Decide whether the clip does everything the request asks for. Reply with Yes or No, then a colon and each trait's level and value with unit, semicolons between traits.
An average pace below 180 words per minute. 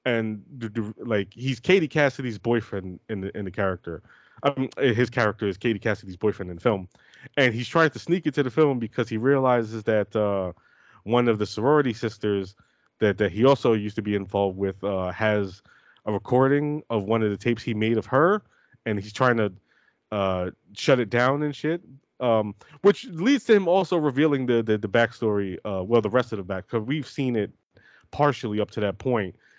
No: average, 200 wpm